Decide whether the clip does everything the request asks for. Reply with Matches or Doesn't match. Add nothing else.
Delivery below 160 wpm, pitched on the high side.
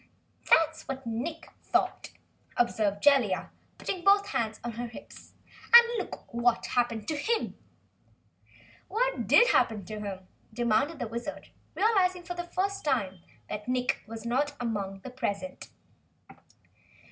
Matches